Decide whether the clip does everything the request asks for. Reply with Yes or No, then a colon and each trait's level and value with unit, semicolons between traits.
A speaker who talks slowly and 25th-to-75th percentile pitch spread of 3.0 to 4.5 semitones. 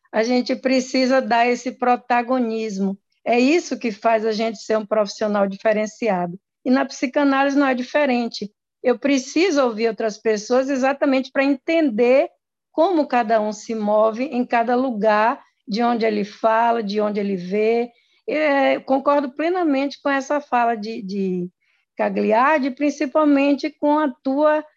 No: average, 145 wpm; average, 4.0 semitones